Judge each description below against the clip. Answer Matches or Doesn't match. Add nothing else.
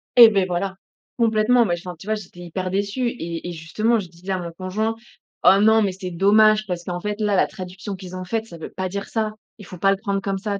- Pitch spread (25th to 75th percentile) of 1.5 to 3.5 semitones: Matches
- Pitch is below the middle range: Doesn't match